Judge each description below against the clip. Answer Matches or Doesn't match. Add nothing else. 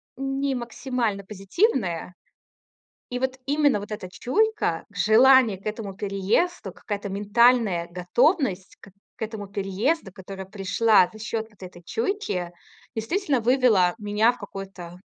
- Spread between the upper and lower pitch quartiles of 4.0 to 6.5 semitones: Matches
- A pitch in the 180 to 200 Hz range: Doesn't match